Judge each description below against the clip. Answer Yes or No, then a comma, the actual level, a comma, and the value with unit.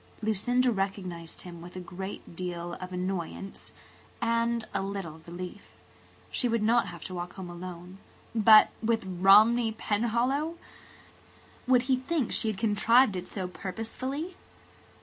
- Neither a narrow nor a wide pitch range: Yes, average, 4.3 semitones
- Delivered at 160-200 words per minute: No, slow, 135 wpm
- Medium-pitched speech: No, high, 200 Hz